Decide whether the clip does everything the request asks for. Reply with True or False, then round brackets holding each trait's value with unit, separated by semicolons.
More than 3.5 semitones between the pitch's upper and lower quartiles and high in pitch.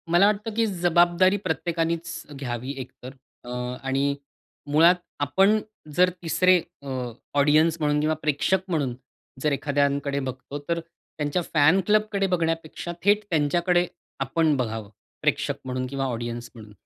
False (4.2 semitones; 155 Hz)